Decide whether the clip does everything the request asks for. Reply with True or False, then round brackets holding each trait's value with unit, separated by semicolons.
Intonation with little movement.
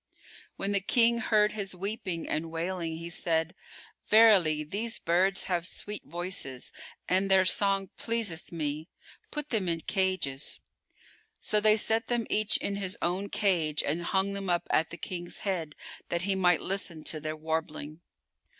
False (3.6 semitones)